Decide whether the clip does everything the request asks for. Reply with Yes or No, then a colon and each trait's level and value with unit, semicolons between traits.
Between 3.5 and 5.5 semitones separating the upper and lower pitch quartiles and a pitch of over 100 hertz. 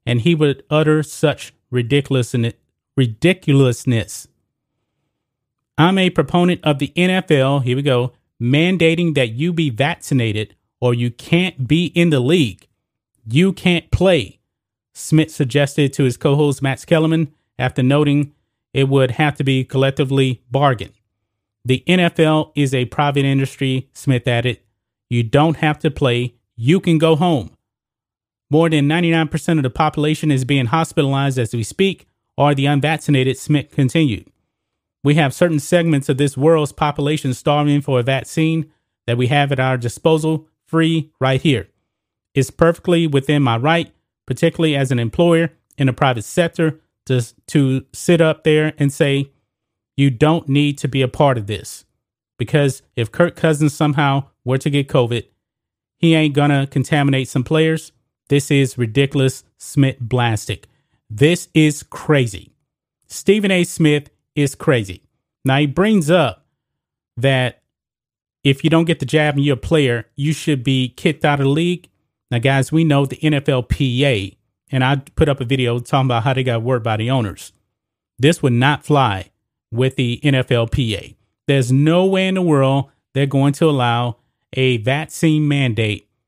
Yes: average, 3.8 semitones; medium, 140 Hz